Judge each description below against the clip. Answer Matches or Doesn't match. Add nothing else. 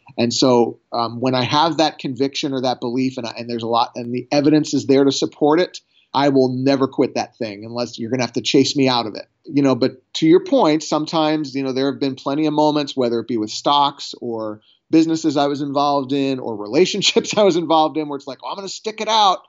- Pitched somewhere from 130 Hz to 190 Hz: Matches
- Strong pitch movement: Doesn't match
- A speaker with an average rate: Doesn't match